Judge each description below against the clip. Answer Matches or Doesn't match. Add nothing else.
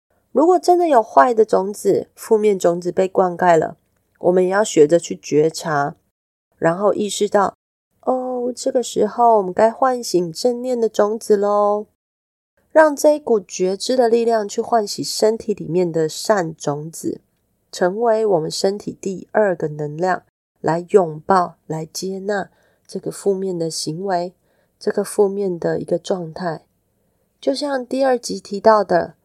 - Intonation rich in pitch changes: Doesn't match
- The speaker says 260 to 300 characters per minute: Doesn't match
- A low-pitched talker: Doesn't match